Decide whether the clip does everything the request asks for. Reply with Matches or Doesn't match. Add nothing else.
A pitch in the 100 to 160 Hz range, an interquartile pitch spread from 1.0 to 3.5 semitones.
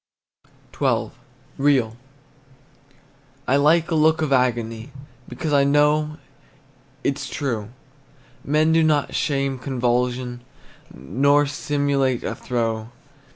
Matches